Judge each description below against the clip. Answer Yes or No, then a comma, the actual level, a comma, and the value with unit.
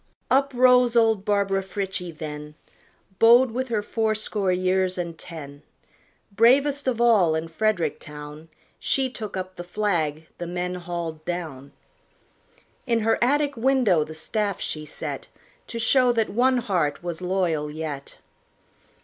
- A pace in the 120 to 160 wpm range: Yes, average, 140 wpm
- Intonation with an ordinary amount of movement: No, wide, 6.1 semitones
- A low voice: No, high, 190 Hz